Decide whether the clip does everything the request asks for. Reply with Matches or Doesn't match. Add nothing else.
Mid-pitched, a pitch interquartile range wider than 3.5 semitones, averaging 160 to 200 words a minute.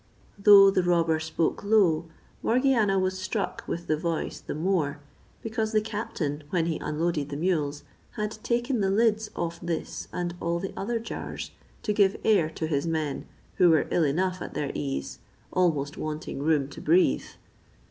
Matches